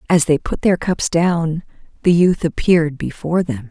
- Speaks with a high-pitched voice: No, medium, 165 Hz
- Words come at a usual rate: Yes, average, 180 wpm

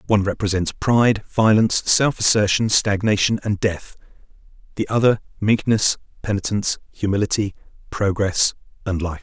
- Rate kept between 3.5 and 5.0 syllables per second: No, 5.2 syllables/s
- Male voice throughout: Yes, male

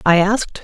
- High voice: Yes, high, 195 Hz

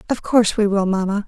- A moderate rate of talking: No, fast, 235 wpm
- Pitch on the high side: Yes, high, 205 Hz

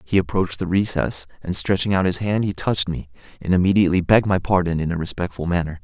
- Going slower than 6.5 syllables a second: No, 6.6 syllables/s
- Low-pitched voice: Yes, very low, 90 Hz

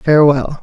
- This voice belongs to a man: Yes, male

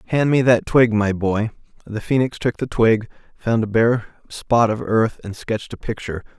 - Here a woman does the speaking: No, male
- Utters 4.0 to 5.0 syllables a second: Yes, 4.8 syllables/s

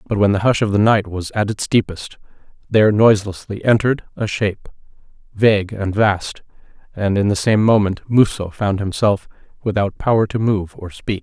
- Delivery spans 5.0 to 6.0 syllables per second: Yes, 5.2 syllables/s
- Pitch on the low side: Yes, low, 105 Hz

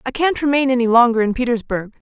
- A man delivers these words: No, female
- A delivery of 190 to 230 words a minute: Yes, average, 200 wpm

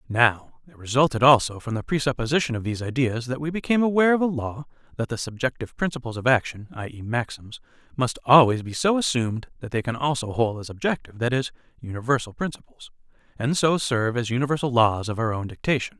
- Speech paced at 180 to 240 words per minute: Yes, average, 195 wpm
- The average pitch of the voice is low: Yes, low, 125 Hz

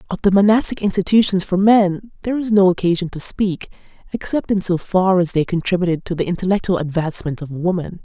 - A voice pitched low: No, medium, 185 Hz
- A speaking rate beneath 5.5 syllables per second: No, 6.0 syllables/s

